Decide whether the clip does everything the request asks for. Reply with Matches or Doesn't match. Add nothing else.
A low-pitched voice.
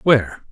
Matches